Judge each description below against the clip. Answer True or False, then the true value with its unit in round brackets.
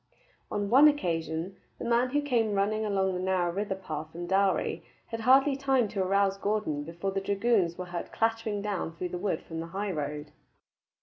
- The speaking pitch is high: True (195 Hz)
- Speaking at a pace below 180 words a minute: False (190 wpm)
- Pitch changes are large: False (4.2 semitones)